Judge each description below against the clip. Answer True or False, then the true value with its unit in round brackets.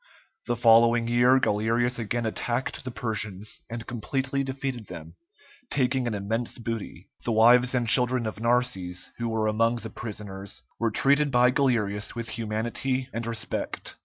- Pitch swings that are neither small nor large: False (2.2 semitones)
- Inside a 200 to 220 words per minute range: False (150 wpm)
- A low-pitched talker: True (115 Hz)